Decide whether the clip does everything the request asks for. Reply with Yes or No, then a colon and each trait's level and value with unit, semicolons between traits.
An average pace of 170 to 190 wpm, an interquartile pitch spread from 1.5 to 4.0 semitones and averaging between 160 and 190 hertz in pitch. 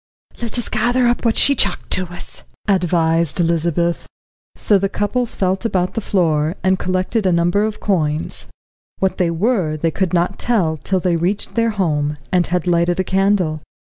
Yes: average, 175 wpm; average, 3.3 semitones; medium, 185 Hz